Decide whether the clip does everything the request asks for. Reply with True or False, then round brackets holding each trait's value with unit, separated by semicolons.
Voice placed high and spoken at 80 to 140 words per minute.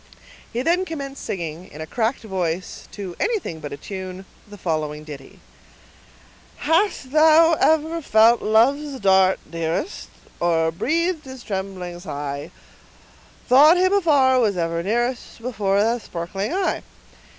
True (215 Hz; 135 wpm)